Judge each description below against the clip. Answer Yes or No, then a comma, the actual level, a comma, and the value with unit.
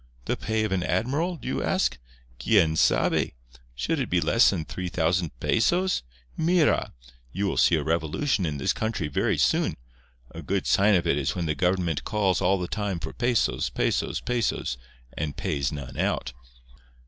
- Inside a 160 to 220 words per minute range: Yes, average, 175 wpm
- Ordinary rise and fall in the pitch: No, wide, 6.0 semitones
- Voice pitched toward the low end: Yes, very low, 90 Hz